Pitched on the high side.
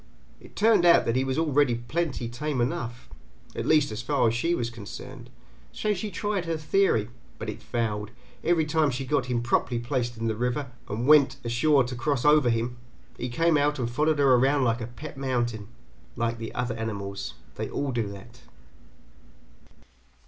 No: low, 125 Hz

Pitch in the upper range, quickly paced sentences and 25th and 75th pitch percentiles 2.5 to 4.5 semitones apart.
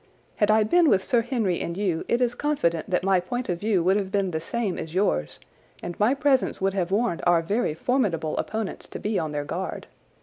No: high, 195 Hz; fast, 225 wpm; average, 5.2 semitones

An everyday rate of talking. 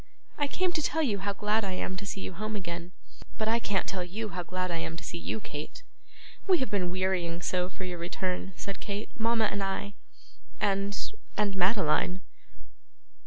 Yes: average, 195 wpm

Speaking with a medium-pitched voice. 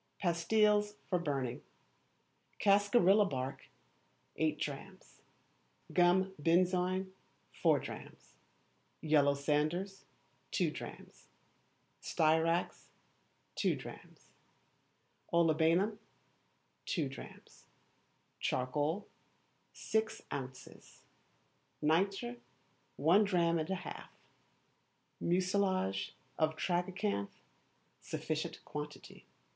Yes: medium, 175 Hz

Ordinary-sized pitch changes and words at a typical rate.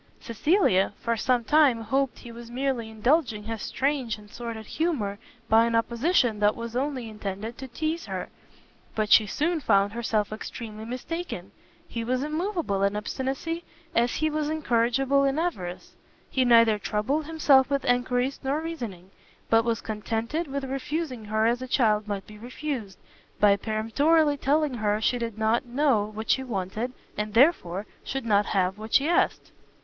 Yes: average, 4.5 semitones; average, 165 wpm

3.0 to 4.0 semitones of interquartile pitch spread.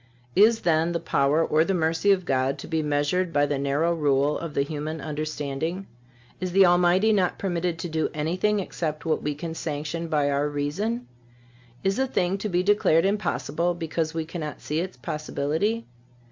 Yes: average, 3.4 semitones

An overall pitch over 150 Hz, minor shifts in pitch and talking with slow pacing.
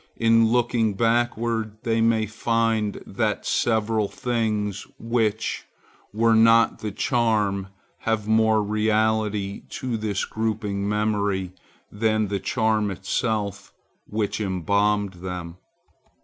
No: low, 110 Hz; narrow, 1.8 semitones; slow, 105 wpm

